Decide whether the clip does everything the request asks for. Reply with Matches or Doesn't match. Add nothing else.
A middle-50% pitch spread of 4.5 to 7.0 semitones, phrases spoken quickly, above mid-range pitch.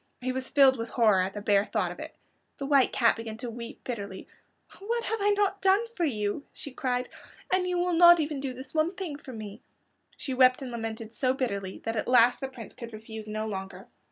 Matches